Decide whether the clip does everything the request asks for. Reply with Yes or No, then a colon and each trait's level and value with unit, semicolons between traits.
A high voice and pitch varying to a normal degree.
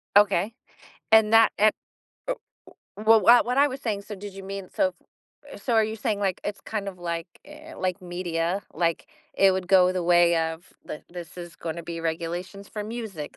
Yes: high, 195 Hz; average, 3.9 semitones